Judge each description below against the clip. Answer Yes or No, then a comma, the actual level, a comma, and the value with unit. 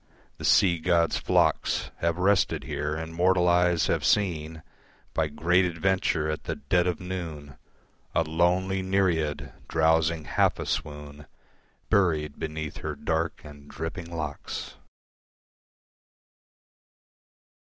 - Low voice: Yes, very low, 80 Hz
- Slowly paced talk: Yes, slow, 115 wpm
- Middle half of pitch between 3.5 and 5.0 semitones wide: No, narrow, 2.5 semitones